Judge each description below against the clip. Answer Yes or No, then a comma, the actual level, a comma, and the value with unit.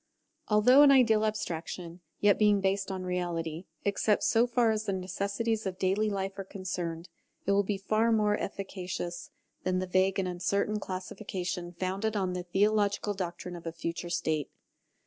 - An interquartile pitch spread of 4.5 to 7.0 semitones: No, average, 2.7 semitones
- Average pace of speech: Yes, average, 165 wpm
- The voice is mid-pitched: No, high, 195 Hz